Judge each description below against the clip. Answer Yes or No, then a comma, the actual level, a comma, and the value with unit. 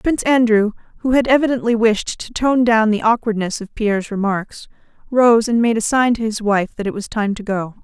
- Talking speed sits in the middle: No, fast, 215 wpm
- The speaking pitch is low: No, high, 225 Hz